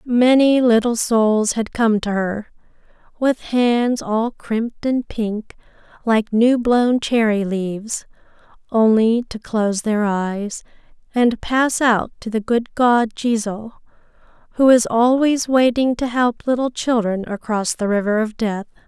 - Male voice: No, female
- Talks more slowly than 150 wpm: Yes, average, 140 wpm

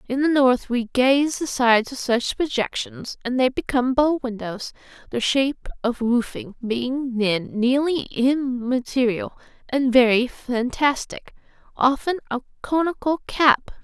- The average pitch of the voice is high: Yes, very high, 260 Hz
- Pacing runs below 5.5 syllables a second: Yes, 4.2 syllables/s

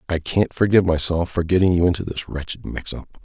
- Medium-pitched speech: No, very low, 85 Hz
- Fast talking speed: Yes, fast, 220 wpm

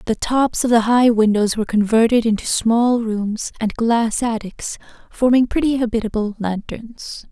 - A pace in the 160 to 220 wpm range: No, average, 150 wpm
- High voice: Yes, high, 230 Hz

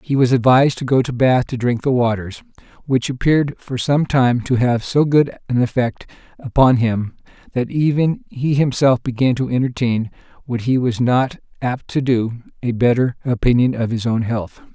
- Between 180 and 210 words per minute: Yes, average, 185 wpm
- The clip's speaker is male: Yes, male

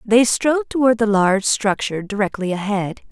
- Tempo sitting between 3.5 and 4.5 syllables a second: No, 5.5 syllables/s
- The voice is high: Yes, high, 215 Hz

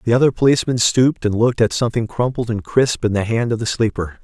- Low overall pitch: Yes, low, 115 Hz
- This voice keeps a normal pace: No, fast, 240 wpm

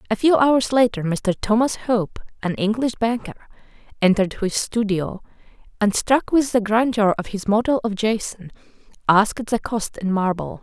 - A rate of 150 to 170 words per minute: Yes, average, 160 wpm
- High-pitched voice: Yes, high, 220 Hz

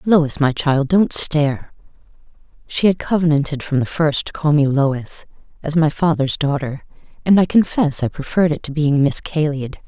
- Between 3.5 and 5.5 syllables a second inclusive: Yes, 5.0 syllables/s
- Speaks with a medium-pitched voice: Yes, medium, 150 Hz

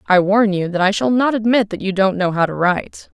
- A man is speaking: No, female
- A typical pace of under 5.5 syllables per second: No, 5.7 syllables/s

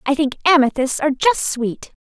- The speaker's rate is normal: Yes, average, 175 wpm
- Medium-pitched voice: No, very high, 285 Hz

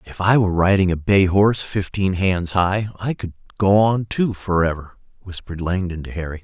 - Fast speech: No, average, 185 wpm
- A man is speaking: Yes, male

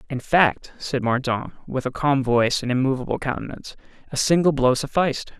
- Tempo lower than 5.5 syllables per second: No, 5.6 syllables/s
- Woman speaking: No, male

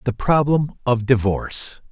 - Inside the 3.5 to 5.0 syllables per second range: Yes, 4.5 syllables/s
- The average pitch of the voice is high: No, low, 125 Hz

